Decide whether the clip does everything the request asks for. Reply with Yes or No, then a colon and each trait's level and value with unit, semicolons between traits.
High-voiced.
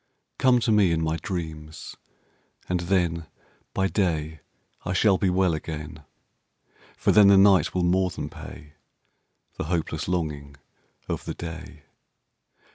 No: very low, 85 Hz